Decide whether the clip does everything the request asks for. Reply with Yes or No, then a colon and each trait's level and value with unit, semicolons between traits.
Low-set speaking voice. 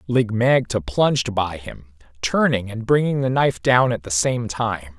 Yes: low, 115 Hz